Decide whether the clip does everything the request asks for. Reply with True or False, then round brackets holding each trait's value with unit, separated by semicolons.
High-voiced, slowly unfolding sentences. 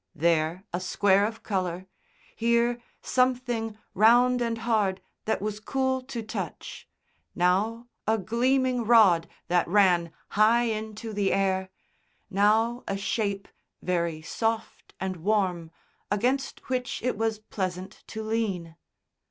True (215 Hz; 120 wpm)